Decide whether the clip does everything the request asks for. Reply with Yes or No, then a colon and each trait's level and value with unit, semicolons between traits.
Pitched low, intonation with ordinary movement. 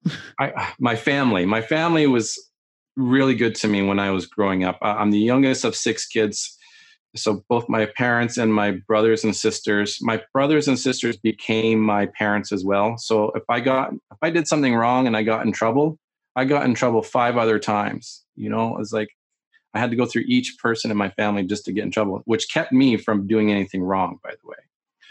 Yes: low, 110 Hz; average, 3.4 semitones